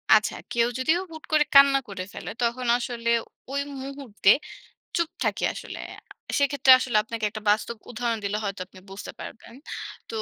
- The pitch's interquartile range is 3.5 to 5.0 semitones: Yes, average, 4.4 semitones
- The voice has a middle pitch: No, high, 235 Hz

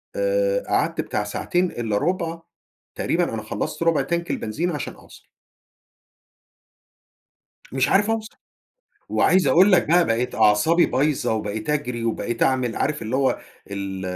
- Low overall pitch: No, medium, 150 Hz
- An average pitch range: No, wide, 7.5 semitones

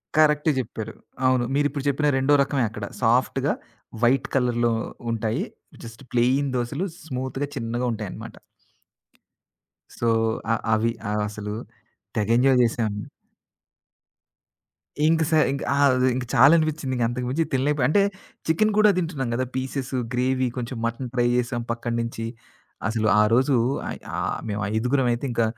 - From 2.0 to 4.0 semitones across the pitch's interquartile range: Yes, average, 3.0 semitones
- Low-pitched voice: Yes, low, 125 Hz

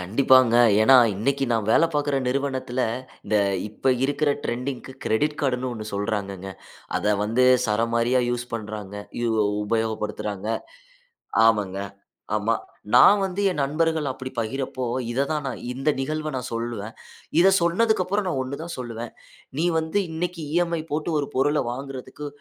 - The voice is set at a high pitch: No, low, 130 Hz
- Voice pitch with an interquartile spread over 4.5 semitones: Yes, average, 4.9 semitones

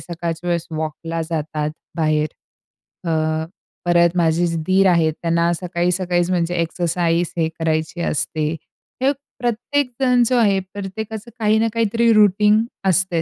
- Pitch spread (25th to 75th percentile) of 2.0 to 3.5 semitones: No, average, 4.1 semitones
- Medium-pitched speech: Yes, medium, 175 Hz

